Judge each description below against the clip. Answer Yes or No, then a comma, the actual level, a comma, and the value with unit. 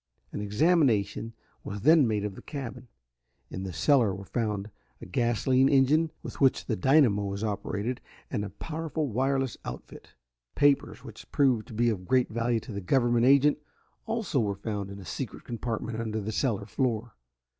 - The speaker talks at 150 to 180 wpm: Yes, average, 170 wpm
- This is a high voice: No, low, 115 Hz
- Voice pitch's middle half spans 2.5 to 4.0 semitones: No, average, 4.6 semitones